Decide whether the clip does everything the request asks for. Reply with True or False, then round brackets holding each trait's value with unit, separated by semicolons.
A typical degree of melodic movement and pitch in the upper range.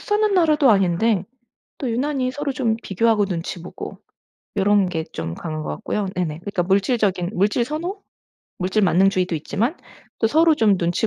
False (6.0 semitones; 205 Hz)